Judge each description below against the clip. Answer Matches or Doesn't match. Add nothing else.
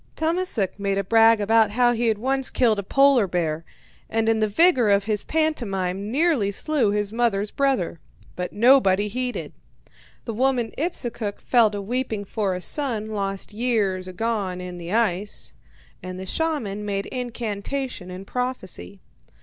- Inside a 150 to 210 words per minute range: Matches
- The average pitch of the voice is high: Matches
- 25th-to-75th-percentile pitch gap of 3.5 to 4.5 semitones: Matches